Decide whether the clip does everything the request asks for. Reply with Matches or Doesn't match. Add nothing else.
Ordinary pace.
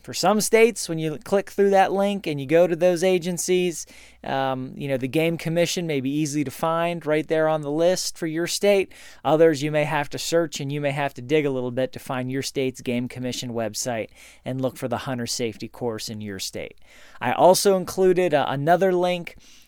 Doesn't match